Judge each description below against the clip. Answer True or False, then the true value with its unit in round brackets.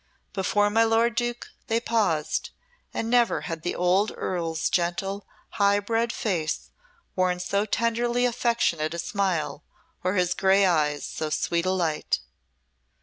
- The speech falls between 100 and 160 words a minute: True (140 wpm)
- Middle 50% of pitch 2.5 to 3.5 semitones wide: False (4.9 semitones)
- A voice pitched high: True (195 Hz)